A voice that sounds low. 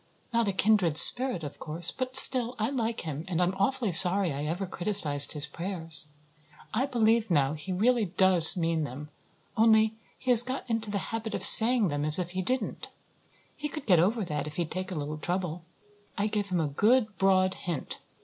No: high, 190 Hz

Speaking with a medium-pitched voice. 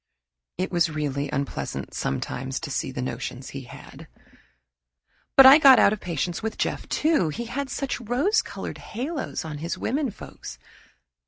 Yes: medium, 180 Hz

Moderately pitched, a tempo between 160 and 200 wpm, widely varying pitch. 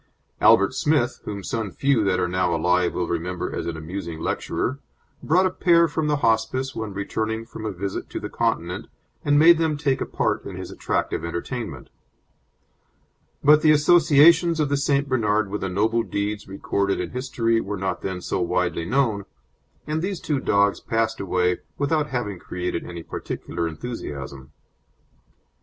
No: low, 110 Hz; average, 165 wpm; wide, 7.6 semitones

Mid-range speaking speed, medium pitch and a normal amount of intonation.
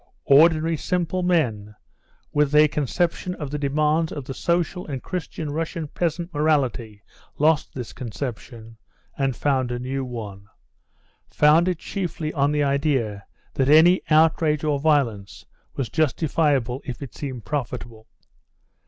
No: slow, 130 wpm; medium, 145 Hz; average, 4.0 semitones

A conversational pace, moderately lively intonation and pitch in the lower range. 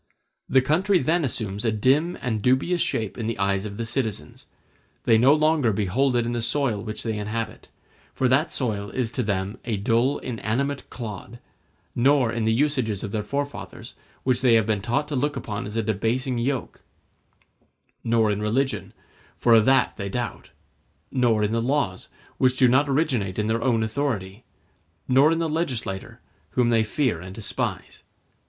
Yes: average, 175 wpm; average, 3.8 semitones; low, 120 Hz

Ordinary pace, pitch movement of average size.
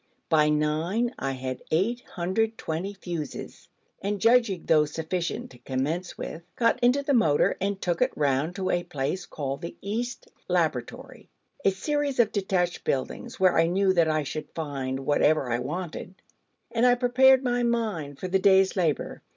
No: average, 160 wpm; wide, 6.6 semitones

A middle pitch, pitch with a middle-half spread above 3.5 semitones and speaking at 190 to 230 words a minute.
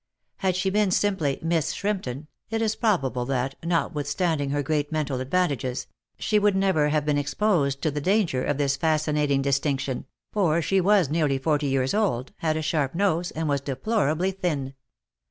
No: medium, 155 Hz; average, 5.0 semitones; average, 170 wpm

